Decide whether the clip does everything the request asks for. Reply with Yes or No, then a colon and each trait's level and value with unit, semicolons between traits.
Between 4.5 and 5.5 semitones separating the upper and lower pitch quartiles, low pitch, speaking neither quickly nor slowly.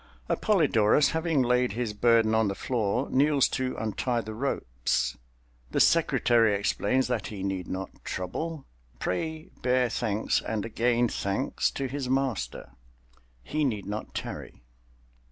No: average, 4.8 semitones; low, 115 Hz; slow, 130 wpm